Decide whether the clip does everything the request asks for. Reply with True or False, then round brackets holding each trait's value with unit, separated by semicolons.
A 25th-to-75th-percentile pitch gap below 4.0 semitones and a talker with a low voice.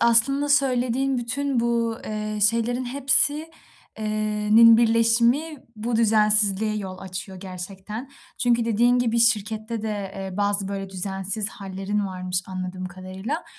False (3.5 semitones; 220 Hz)